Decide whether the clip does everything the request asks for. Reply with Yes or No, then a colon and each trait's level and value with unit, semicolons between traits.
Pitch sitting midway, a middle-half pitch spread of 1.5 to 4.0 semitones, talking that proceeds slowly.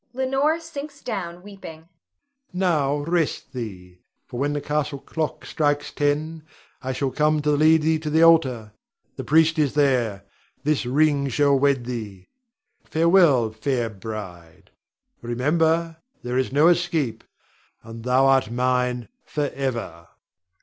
No: medium, 145 Hz; average, 4.7 semitones; slow, 130 wpm